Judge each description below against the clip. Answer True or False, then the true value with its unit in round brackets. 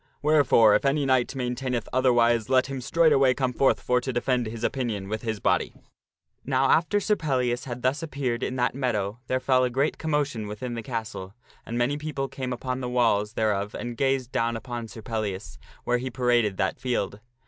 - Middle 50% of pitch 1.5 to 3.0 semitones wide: True (2.7 semitones)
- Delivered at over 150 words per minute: True (195 wpm)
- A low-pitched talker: True (125 Hz)